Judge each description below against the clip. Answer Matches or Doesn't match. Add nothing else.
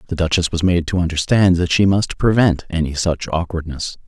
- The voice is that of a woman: Doesn't match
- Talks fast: Doesn't match